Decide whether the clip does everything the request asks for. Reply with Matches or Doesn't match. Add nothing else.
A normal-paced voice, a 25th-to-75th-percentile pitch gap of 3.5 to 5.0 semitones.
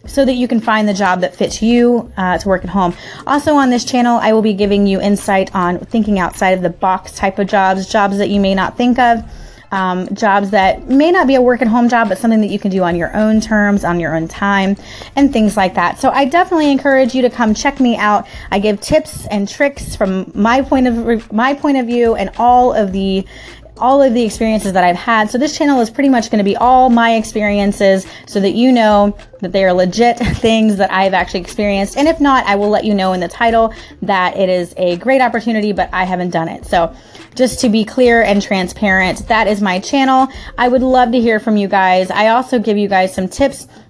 Doesn't match